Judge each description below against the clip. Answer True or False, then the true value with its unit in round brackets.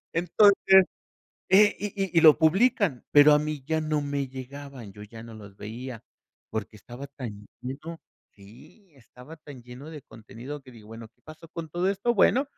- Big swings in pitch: True (5.9 semitones)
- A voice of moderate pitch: True (145 Hz)